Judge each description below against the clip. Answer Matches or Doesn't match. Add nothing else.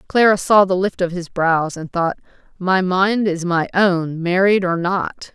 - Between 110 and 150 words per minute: Doesn't match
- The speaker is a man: Doesn't match